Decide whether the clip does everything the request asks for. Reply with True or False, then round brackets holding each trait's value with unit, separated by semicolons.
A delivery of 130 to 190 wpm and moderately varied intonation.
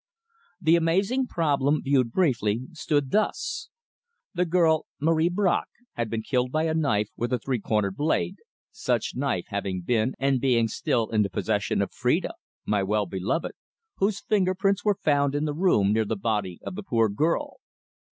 False (170 wpm; 7.4 semitones)